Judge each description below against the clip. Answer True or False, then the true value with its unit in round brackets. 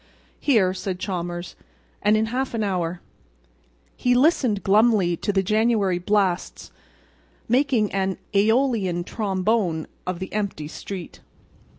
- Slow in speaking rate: True (115 wpm)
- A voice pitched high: True (200 Hz)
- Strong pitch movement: False (3.5 semitones)